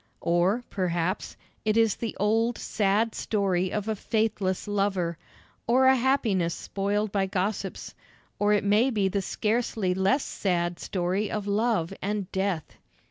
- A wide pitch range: No, average, 2.7 semitones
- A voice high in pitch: Yes, high, 200 Hz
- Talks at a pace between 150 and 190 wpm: No, average, 140 wpm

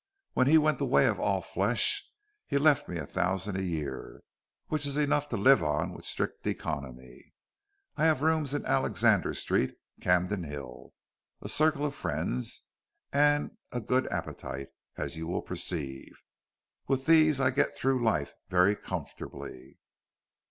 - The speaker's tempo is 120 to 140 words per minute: No, average, 150 wpm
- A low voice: Yes, low, 110 Hz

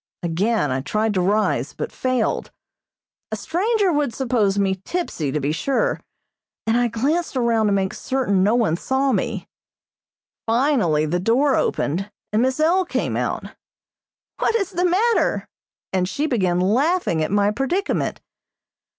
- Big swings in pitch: Yes, wide, 7.2 semitones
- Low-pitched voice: No, high, 230 Hz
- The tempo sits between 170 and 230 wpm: No, average, 150 wpm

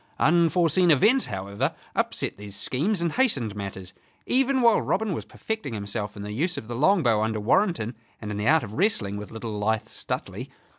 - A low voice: Yes, low, 120 Hz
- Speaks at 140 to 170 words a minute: No, average, 185 wpm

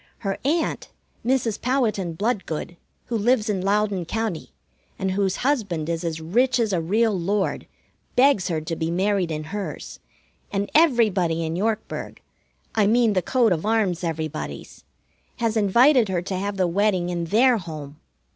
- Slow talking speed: No, average, 155 wpm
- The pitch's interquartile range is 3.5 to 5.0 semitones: Yes, average, 4.7 semitones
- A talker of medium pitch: No, high, 200 Hz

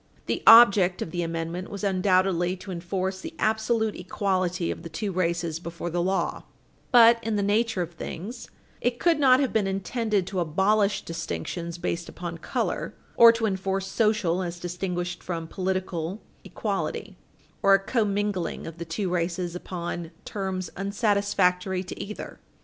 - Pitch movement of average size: Yes, average, 3.0 semitones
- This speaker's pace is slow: No, average, 155 wpm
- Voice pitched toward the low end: No, medium, 185 Hz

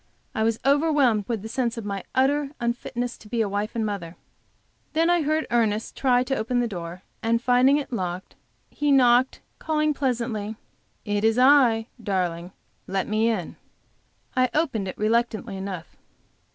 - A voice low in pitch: No, high, 230 Hz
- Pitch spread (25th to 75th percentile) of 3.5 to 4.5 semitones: Yes, average, 4.0 semitones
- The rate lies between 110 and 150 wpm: No, average, 165 wpm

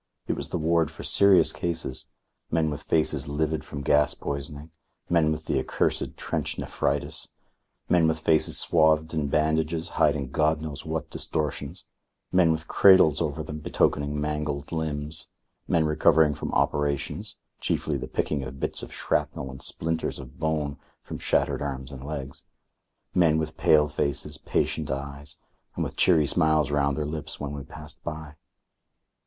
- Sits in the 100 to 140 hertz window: No, very low, 75 Hz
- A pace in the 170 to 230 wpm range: No, average, 155 wpm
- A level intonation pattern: Yes, narrow, 1.7 semitones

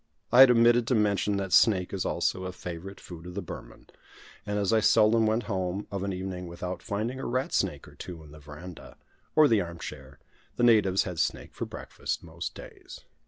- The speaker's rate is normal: No, fast, 210 wpm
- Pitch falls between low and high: No, low, 100 Hz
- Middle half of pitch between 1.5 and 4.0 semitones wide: Yes, average, 3.7 semitones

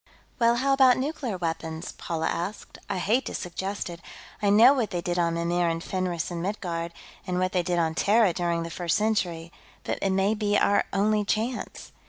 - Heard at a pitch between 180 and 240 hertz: Yes, medium, 185 Hz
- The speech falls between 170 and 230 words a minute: Yes, average, 200 wpm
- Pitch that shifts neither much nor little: Yes, average, 3.9 semitones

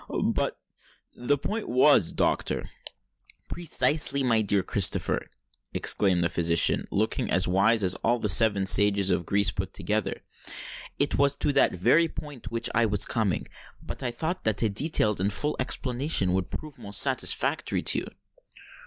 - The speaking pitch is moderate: No, low, 110 Hz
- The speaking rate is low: No, average, 155 wpm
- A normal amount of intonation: No, wide, 6.2 semitones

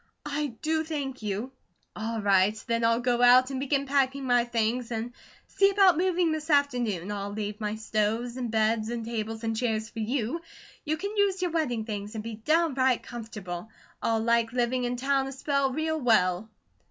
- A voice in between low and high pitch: No, high, 240 Hz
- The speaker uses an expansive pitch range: No, average, 4.1 semitones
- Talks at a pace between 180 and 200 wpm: Yes, average, 185 wpm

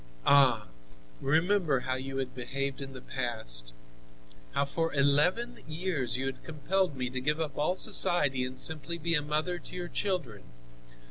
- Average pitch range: Yes, average, 4.5 semitones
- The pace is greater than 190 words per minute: No, average, 160 wpm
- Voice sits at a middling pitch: Yes, medium, 145 Hz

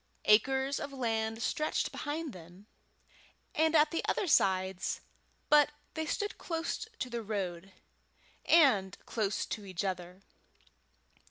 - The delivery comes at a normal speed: No, slow, 120 wpm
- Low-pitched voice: No, high, 225 Hz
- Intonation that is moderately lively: No, wide, 7.7 semitones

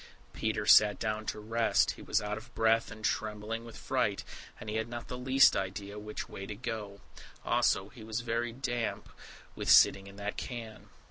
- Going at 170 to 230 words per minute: Yes, average, 190 wpm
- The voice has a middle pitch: No, low, 110 Hz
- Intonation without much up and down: Yes, narrow, 2.0 semitones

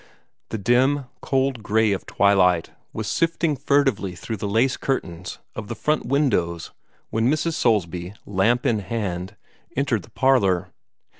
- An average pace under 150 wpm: Yes, average, 140 wpm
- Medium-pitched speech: No, low, 110 Hz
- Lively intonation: Yes, wide, 6.0 semitones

